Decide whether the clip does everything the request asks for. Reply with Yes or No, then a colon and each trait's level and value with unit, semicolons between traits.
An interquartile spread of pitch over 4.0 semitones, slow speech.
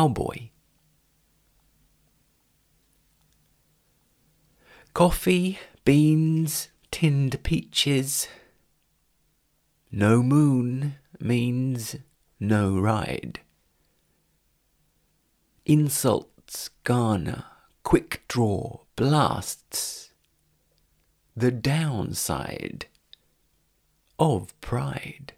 Yes: average, 5.0 semitones; slow, 45 wpm